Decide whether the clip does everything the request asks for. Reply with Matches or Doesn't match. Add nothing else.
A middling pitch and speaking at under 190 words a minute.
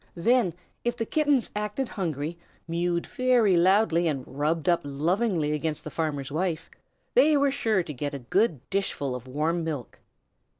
Matches